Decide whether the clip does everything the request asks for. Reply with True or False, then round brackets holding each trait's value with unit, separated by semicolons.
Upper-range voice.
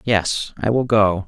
False (105 Hz)